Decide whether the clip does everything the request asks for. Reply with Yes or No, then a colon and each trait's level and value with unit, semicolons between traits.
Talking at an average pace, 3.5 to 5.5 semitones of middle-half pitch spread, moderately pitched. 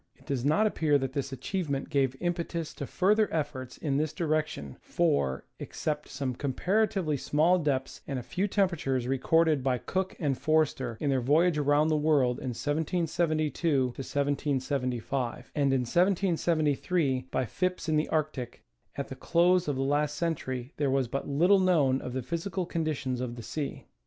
Yes: average, 165 wpm; average, 4.0 semitones; medium, 145 Hz